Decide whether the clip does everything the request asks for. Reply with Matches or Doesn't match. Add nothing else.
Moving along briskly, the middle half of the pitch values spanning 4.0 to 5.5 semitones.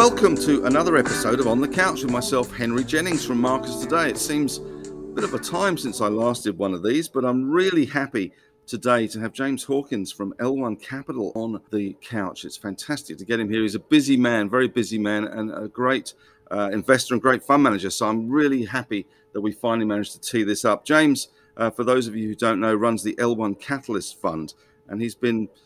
Doesn't match